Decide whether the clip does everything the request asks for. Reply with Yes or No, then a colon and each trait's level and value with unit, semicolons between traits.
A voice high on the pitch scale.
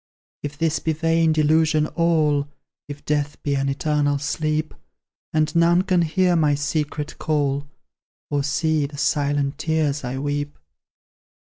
No: medium, 150 Hz